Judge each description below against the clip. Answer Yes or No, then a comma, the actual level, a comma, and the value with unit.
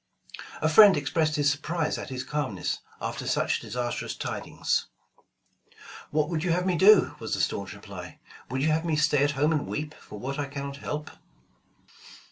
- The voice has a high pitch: No, medium, 150 Hz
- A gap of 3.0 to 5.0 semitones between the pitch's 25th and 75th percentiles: No, narrow, 2.5 semitones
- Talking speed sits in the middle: Yes, average, 175 wpm